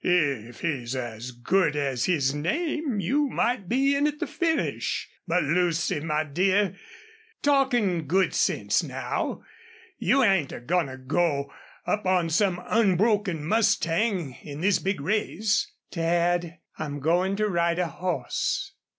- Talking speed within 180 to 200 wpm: No, average, 140 wpm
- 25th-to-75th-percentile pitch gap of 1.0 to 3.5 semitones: No, wide, 5.6 semitones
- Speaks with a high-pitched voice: No, medium, 175 Hz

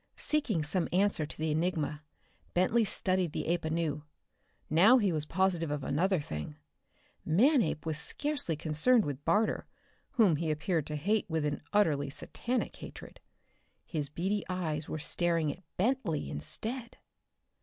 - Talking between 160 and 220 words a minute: No, average, 145 wpm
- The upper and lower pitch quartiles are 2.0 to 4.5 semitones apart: No, average, 5.1 semitones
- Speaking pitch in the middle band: Yes, medium, 165 Hz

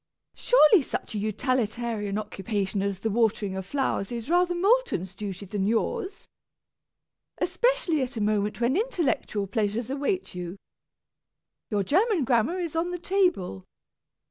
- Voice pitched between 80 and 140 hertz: No, high, 235 Hz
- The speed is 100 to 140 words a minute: Yes, slow, 135 wpm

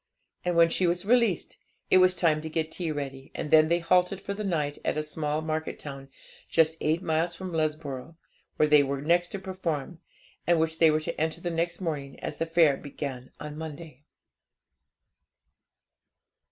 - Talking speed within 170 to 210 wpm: Yes, average, 180 wpm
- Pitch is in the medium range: Yes, medium, 160 Hz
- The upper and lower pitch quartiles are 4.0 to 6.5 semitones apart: No, narrow, 2.4 semitones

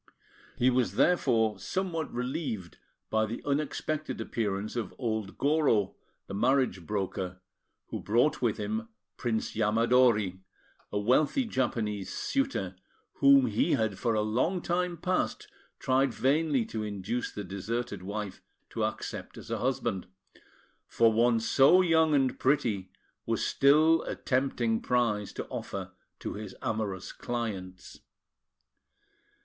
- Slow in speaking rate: Yes, slow, 125 wpm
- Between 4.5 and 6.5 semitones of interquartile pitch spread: Yes, average, 4.8 semitones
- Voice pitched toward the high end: No, low, 115 Hz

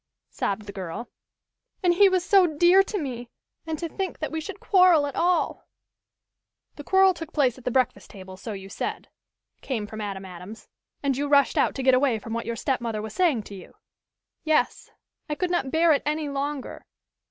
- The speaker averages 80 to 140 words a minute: No, average, 200 wpm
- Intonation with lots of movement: Yes, wide, 7.1 semitones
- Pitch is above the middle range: Yes, very high, 280 Hz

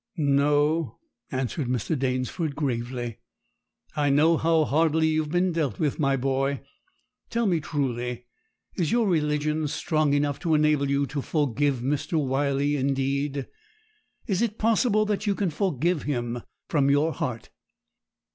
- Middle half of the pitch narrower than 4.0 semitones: Yes, average, 2.9 semitones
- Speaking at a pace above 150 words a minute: No, average, 140 wpm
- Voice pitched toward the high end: No, medium, 145 Hz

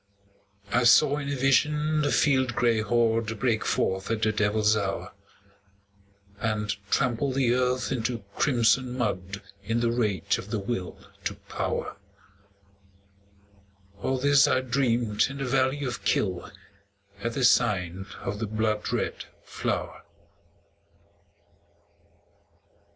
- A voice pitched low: Yes, low, 120 Hz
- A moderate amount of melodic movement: Yes, average, 3.6 semitones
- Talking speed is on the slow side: Yes, slow, 125 wpm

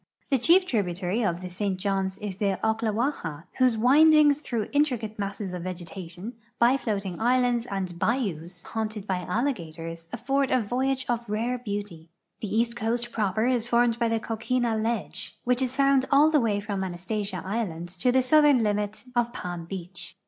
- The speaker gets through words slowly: No, average, 170 wpm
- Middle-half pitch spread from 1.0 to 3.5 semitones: No, average, 4.6 semitones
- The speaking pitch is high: Yes, high, 220 Hz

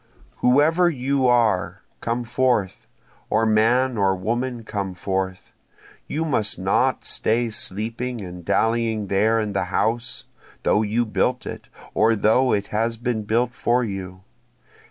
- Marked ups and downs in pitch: No, average, 3.3 semitones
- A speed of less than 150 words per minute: Yes, slow, 135 wpm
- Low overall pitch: Yes, low, 115 Hz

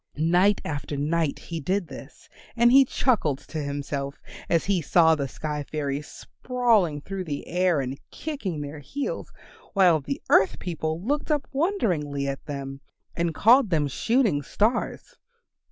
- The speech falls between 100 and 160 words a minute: Yes, average, 150 wpm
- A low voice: No, medium, 165 Hz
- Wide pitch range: Yes, wide, 6.3 semitones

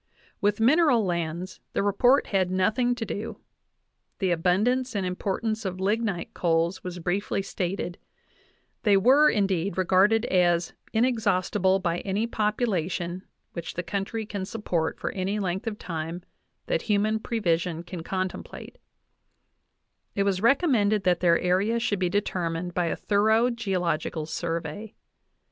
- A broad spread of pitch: No, average, 3.6 semitones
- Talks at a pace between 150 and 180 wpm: No, slow, 135 wpm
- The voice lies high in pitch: Yes, high, 195 Hz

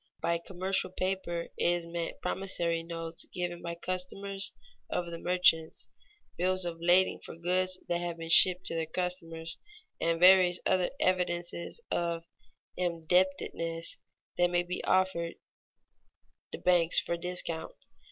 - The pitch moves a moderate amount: No, narrow, 1.5 semitones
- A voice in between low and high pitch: Yes, medium, 175 Hz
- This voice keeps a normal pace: No, slow, 130 wpm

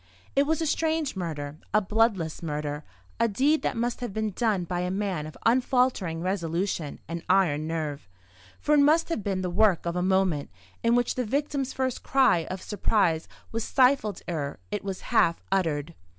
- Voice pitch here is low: No, high, 195 Hz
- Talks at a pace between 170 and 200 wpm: Yes, average, 180 wpm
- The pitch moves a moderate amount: No, wide, 6.6 semitones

